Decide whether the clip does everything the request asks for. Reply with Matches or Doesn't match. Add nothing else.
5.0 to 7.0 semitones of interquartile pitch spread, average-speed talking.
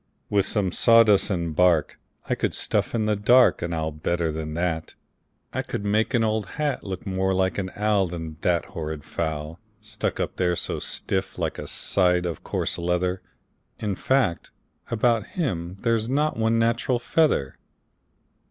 Doesn't match